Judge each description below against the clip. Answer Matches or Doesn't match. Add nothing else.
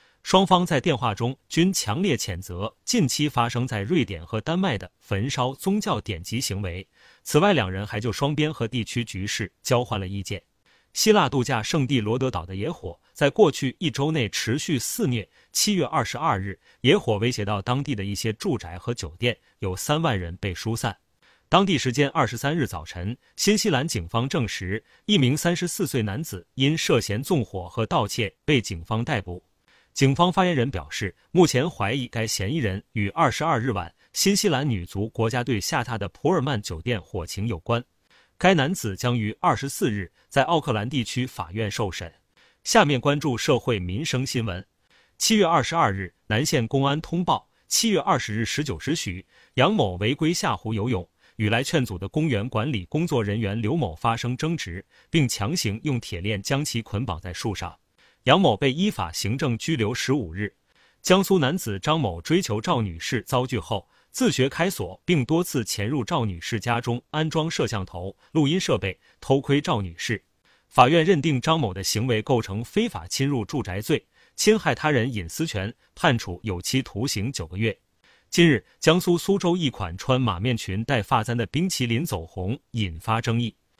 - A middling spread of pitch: Doesn't match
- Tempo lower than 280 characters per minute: Matches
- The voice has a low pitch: Matches